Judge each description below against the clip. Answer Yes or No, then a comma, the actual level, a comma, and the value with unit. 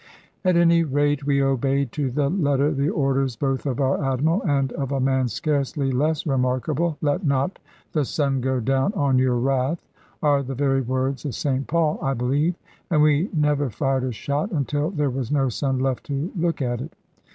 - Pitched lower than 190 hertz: Yes, medium, 140 Hz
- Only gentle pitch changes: Yes, narrow, 2.1 semitones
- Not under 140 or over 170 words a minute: No, average, 190 wpm